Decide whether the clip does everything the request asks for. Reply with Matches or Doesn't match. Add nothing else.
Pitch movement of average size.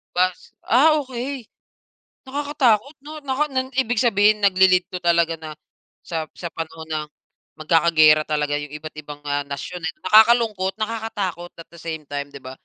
Doesn't match